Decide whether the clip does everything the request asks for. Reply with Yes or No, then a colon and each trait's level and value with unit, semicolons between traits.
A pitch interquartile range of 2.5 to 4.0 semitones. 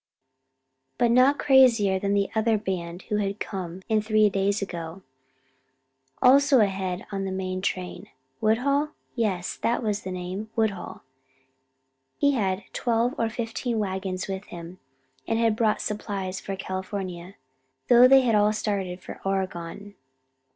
Yes: average, 3.2 semitones